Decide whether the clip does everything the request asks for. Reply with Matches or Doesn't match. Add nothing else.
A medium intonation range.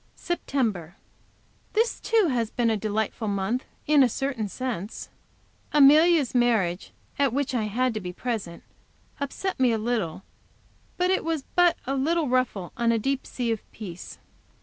Matches